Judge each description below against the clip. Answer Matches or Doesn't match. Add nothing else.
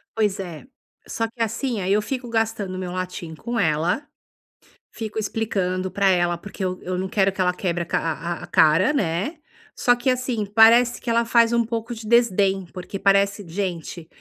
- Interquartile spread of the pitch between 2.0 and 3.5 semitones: Doesn't match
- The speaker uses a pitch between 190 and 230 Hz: Matches